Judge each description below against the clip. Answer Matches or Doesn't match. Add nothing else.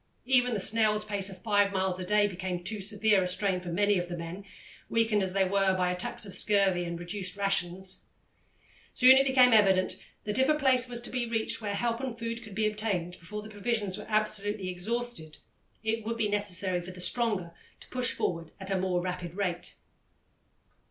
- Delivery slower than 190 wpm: Doesn't match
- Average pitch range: Matches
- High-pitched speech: Matches